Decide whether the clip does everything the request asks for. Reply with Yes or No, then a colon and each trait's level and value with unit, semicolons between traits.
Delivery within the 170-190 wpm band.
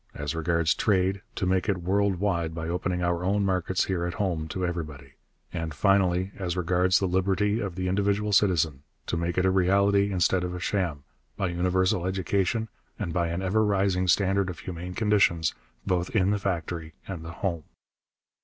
Yes: average, 180 wpm